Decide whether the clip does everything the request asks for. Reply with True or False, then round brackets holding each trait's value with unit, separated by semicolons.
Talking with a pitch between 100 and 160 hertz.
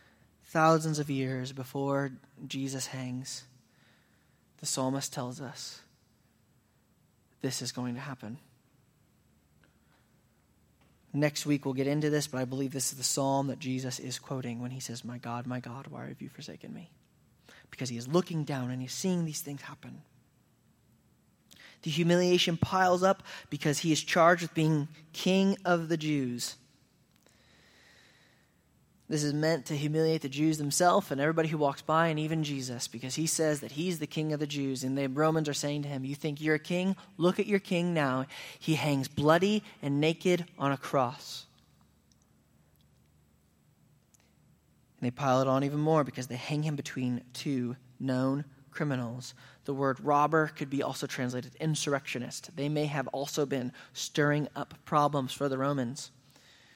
True (140 Hz)